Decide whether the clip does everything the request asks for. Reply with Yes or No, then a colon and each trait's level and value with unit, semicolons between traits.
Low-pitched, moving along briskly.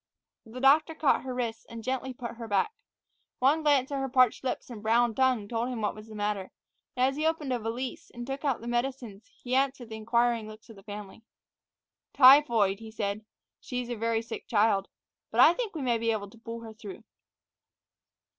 No: high, 235 Hz; fast, 210 wpm